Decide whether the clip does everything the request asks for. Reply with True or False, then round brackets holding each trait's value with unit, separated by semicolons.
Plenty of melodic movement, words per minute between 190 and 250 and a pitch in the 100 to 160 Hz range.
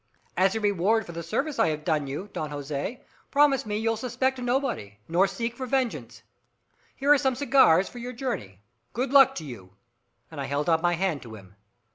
False (8.9 semitones; 200 wpm; 205 Hz)